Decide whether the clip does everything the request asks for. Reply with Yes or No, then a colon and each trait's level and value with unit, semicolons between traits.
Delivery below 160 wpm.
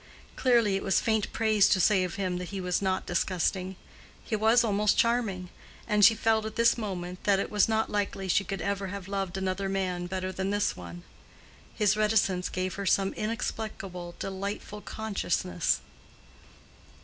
No: average, 170 wpm